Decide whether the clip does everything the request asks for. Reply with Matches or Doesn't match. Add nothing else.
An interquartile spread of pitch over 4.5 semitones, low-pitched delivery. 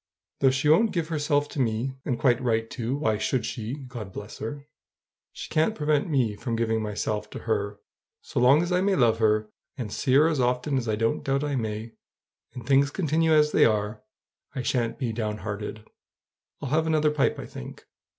Matches